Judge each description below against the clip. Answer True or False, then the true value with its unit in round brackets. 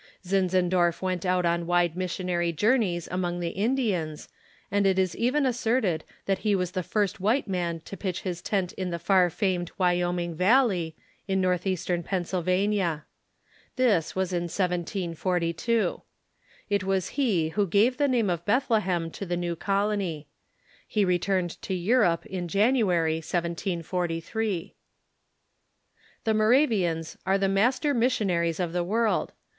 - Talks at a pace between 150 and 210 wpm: False (140 wpm)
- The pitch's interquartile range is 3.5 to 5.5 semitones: False (3.1 semitones)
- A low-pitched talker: False (185 Hz)